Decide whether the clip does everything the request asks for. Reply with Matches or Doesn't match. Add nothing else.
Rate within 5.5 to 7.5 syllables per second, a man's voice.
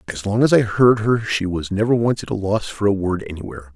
Matches